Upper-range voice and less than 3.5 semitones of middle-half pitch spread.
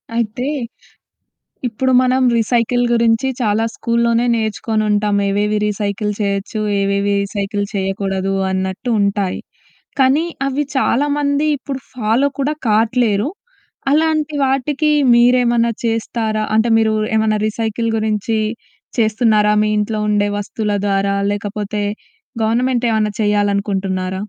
Yes: high, 220 Hz; average, 3.0 semitones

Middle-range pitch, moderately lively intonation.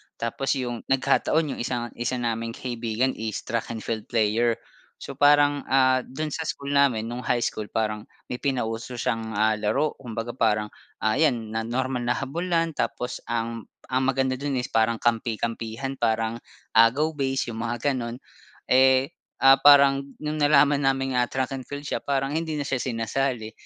No: low, 125 Hz; average, 3.2 semitones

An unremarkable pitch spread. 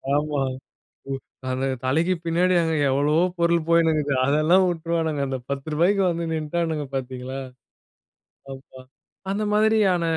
Yes: average, 3.4 semitones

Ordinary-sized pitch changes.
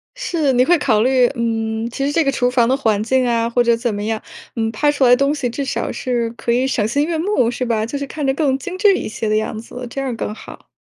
Yes: average, 3.3 semitones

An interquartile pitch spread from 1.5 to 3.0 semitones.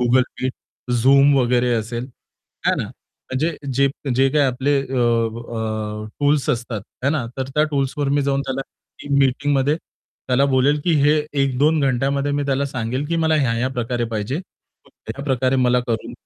Yes: average, 2.7 semitones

